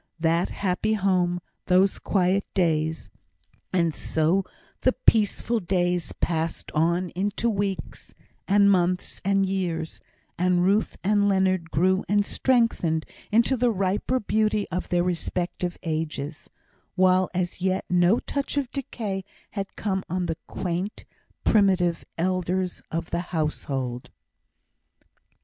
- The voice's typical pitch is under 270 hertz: Yes, medium, 185 Hz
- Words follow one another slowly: Yes, slow, 120 wpm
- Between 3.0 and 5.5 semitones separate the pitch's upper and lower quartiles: No, narrow, 2.5 semitones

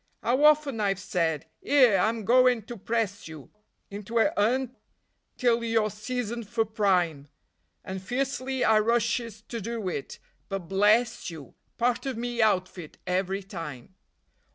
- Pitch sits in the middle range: No, high, 220 Hz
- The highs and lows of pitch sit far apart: No, average, 3.8 semitones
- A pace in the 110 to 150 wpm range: Yes, average, 140 wpm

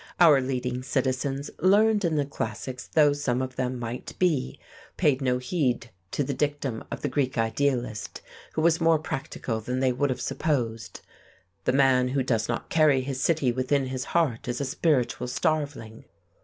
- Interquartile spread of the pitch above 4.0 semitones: No, average, 2.8 semitones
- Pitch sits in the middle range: No, low, 130 Hz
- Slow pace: No, average, 170 wpm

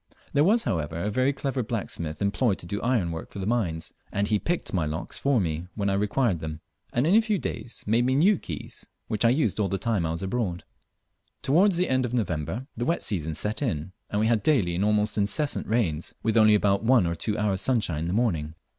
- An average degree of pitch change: No, wide, 6.2 semitones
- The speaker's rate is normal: No, fast, 230 wpm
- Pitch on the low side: Yes, low, 105 Hz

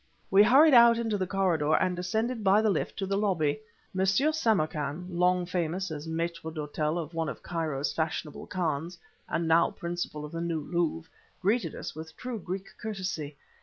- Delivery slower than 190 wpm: Yes, average, 175 wpm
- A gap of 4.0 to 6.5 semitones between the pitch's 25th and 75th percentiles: No, average, 3.5 semitones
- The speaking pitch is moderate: Yes, medium, 175 Hz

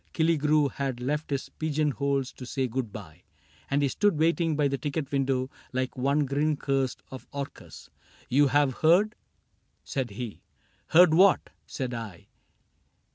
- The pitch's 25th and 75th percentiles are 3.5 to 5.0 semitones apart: No, average, 2.8 semitones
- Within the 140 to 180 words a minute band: Yes, average, 170 wpm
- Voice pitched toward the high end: No, medium, 140 Hz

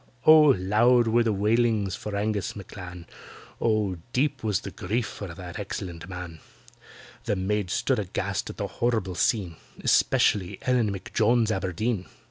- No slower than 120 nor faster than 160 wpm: Yes, average, 140 wpm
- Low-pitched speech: Yes, low, 105 Hz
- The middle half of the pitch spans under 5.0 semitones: Yes, average, 3.7 semitones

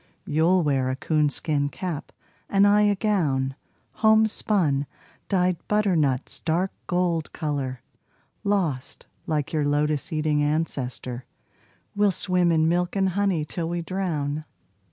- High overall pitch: No, medium, 160 Hz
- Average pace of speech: No, slow, 120 wpm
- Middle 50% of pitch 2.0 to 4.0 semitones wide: No, average, 4.4 semitones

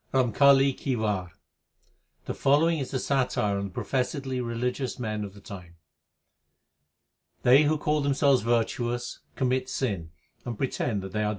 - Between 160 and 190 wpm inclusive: Yes, average, 165 wpm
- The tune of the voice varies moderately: Yes, average, 4.2 semitones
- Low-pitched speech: Yes, low, 125 Hz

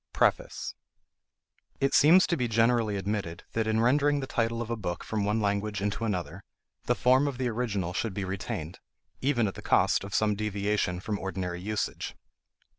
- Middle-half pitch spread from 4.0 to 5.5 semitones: No, average, 3.1 semitones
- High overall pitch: No, low, 105 Hz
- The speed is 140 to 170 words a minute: No, average, 180 wpm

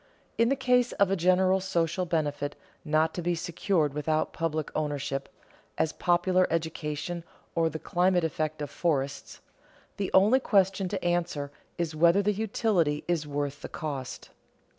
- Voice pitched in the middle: Yes, medium, 170 Hz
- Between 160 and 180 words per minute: No, average, 150 wpm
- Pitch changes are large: No, average, 3.7 semitones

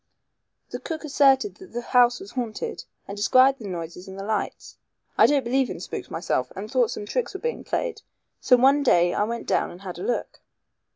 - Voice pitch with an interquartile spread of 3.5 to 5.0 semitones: No, wide, 5.4 semitones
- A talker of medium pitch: No, high, 245 Hz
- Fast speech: Yes, fast, 210 wpm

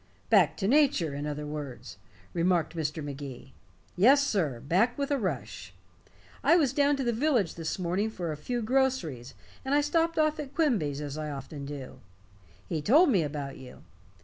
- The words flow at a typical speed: Yes, average, 175 wpm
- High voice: No, medium, 175 Hz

